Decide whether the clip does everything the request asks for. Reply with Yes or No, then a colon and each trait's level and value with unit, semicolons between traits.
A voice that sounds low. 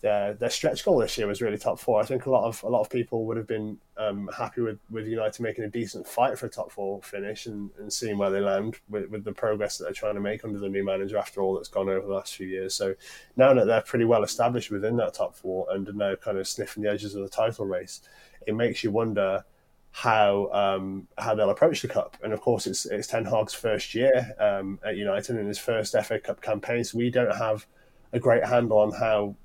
Yes: low, 105 Hz